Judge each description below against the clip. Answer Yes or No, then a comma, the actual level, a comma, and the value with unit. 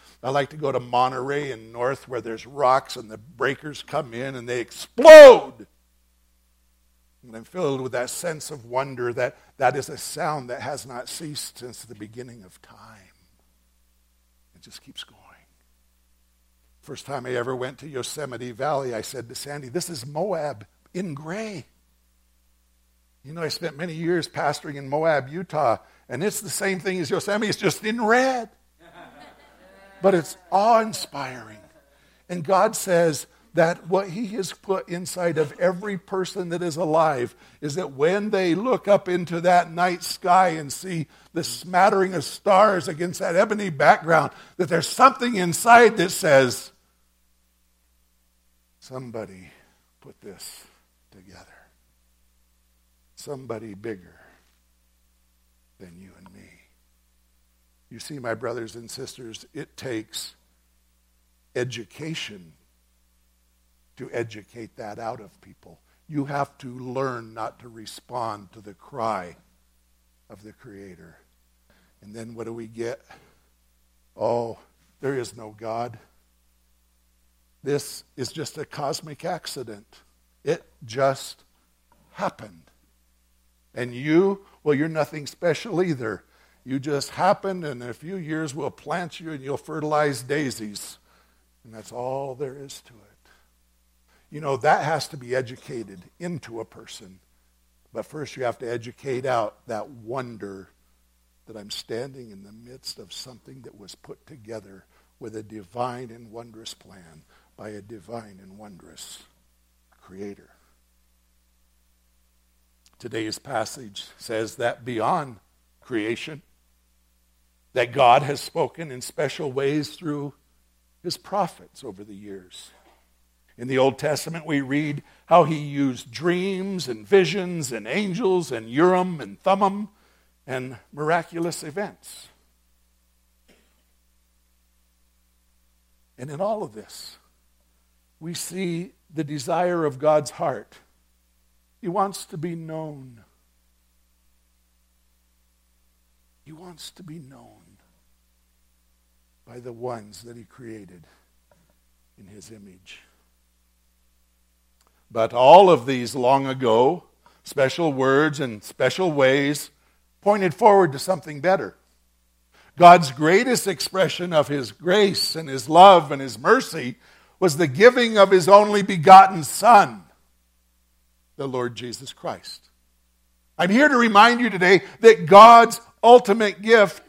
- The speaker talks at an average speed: No, slow, 130 wpm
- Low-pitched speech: Yes, low, 120 Hz